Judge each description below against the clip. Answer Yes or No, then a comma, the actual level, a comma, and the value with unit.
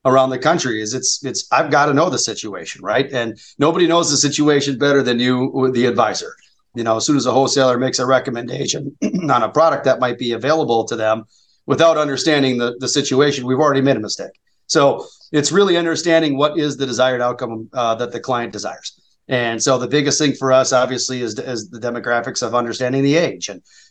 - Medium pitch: No, low, 130 Hz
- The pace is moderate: No, fast, 210 wpm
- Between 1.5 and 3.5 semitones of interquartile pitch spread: Yes, average, 2.8 semitones